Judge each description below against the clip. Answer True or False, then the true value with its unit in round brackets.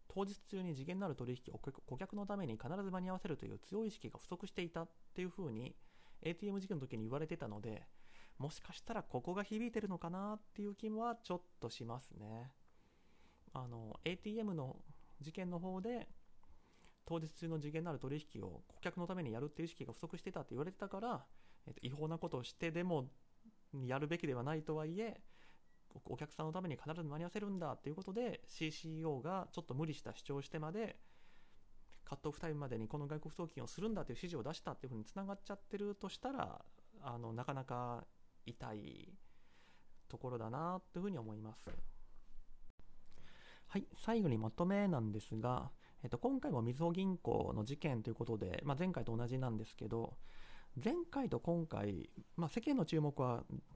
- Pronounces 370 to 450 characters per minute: True (380 characters per minute)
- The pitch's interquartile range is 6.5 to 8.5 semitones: True (7.5 semitones)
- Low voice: False (155 Hz)